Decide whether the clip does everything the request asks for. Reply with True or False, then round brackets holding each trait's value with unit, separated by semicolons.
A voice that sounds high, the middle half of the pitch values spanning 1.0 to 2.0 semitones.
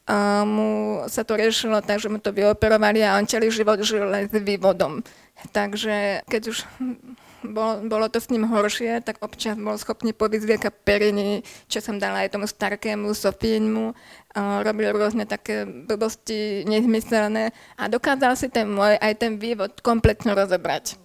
True (215 Hz; 1.4 semitones)